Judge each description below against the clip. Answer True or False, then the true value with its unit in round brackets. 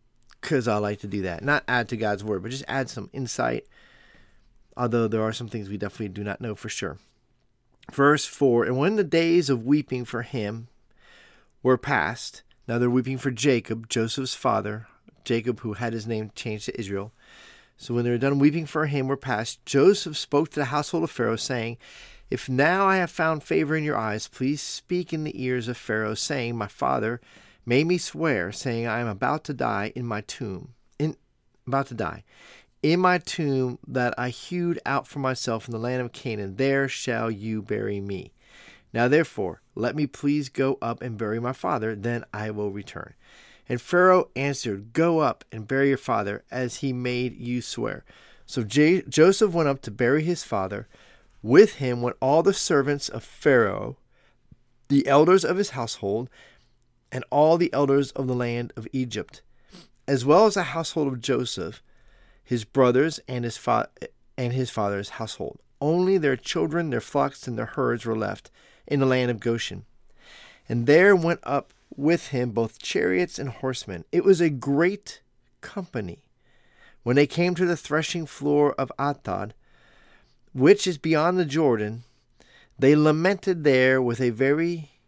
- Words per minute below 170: False (180 wpm)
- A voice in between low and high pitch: False (130 Hz)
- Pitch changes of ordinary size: True (4.3 semitones)